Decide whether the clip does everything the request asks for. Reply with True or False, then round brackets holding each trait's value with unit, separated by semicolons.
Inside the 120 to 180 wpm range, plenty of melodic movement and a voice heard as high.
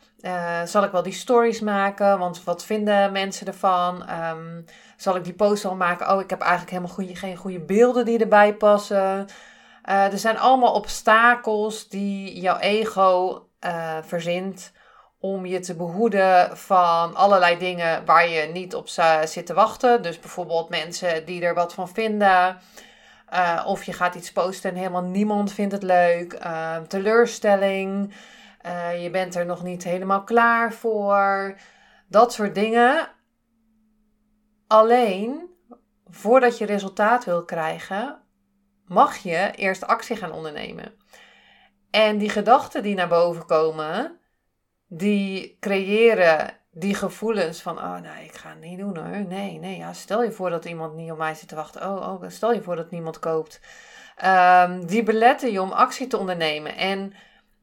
False (160 wpm; 3.4 semitones; 195 Hz)